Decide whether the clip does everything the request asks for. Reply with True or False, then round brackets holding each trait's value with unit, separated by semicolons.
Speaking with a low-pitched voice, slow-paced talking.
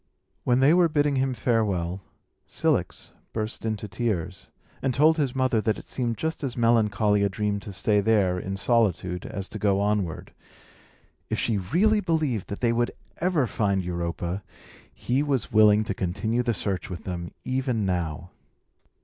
False (110 Hz; 165 wpm)